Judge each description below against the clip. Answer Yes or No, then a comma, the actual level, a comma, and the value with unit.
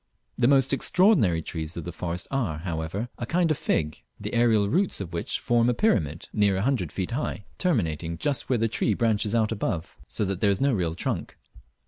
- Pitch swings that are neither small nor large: No, wide, 6.4 semitones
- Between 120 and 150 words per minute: No, fast, 205 wpm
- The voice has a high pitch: No, low, 105 Hz